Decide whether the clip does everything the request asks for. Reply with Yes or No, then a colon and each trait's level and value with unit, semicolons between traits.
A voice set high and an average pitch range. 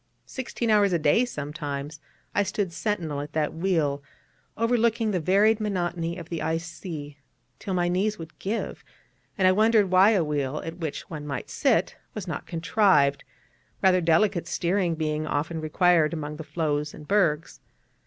No: medium, 170 Hz; average, 4.5 semitones